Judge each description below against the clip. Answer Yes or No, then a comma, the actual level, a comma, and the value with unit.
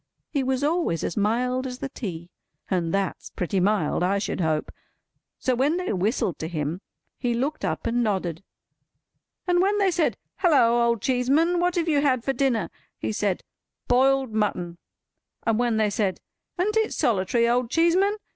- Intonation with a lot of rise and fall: Yes, wide, 6.5 semitones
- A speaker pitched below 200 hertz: No, high, 240 Hz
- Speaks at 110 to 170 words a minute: Yes, average, 165 wpm